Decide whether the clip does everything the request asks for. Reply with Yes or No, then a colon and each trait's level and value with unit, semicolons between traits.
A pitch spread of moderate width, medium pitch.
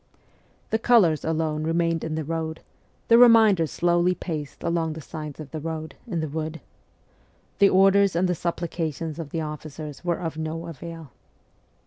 No: narrow, 1.8 semitones; medium, 165 Hz